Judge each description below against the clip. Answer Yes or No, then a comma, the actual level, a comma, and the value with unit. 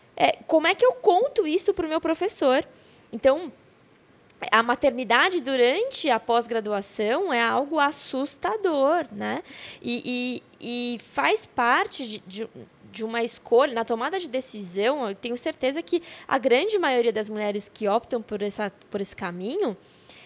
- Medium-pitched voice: No, very high, 250 Hz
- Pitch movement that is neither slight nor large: No, wide, 6.6 semitones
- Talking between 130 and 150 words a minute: Yes, average, 145 wpm